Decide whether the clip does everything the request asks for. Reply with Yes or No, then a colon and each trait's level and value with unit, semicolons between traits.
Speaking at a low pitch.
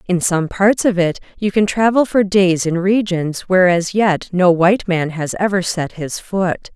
No: medium, 185 Hz